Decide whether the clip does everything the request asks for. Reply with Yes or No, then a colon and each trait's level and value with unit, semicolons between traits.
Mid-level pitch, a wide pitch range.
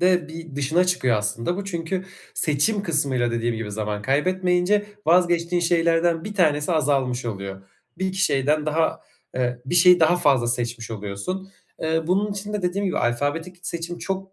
Yes: medium, 165 Hz; wide, 6.2 semitones